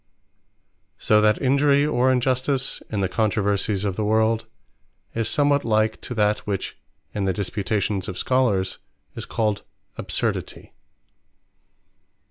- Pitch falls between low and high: No, low, 110 Hz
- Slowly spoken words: Yes, slow, 120 wpm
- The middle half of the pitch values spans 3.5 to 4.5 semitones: Yes, average, 3.9 semitones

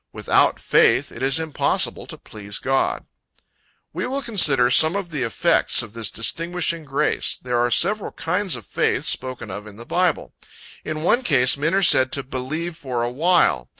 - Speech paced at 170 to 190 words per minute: Yes, average, 180 wpm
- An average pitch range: No, wide, 5.8 semitones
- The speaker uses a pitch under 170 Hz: Yes, medium, 140 Hz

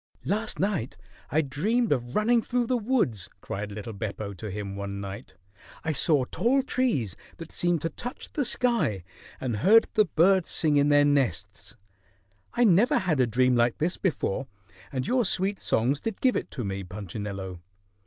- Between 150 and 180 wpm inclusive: Yes, average, 175 wpm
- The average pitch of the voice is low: No, medium, 145 Hz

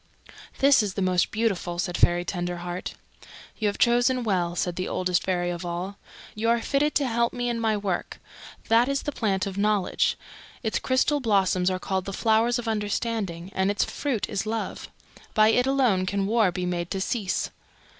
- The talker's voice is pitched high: Yes, high, 205 Hz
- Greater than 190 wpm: No, average, 185 wpm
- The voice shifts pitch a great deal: No, average, 4.2 semitones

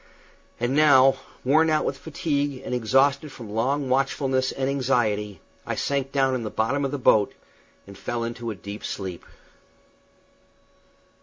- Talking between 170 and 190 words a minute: No, average, 150 wpm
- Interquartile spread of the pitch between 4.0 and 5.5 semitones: No, average, 3.4 semitones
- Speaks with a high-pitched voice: No, low, 130 Hz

